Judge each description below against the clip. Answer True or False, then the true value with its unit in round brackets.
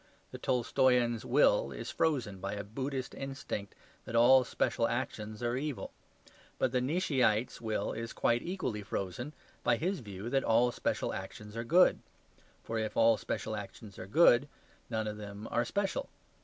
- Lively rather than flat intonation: False (3.7 semitones)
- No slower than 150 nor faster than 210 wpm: True (160 wpm)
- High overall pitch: False (120 Hz)